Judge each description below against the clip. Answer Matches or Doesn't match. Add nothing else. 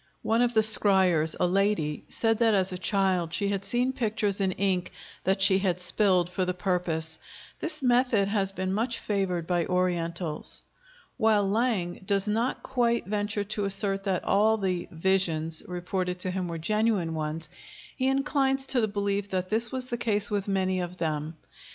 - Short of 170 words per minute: Doesn't match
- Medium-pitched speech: Doesn't match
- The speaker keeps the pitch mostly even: Doesn't match